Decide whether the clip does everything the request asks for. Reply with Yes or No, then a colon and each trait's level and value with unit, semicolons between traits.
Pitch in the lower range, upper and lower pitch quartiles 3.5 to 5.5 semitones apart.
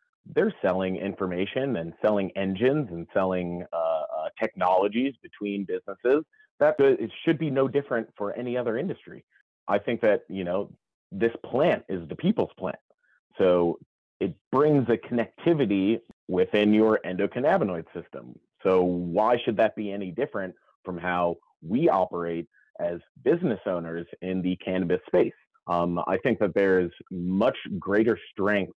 Yes: very low, 95 Hz; average, 4.5 semitones